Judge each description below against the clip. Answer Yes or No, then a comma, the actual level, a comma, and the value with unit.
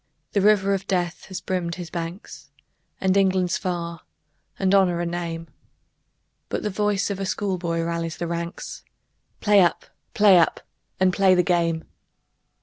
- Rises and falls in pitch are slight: Yes, narrow, 2.3 semitones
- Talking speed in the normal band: Yes, average, 150 wpm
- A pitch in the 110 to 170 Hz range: No, medium, 180 Hz